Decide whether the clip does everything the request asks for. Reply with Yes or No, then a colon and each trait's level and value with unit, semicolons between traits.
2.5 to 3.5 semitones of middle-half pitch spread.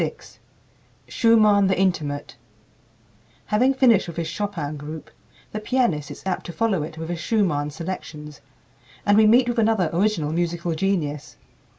No: average, 5.2 semitones